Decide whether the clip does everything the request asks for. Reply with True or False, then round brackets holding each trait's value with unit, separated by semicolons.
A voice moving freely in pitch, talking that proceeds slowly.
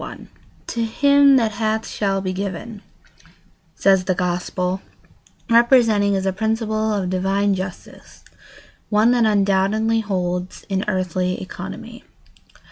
False (2.9 semitones; 120 wpm)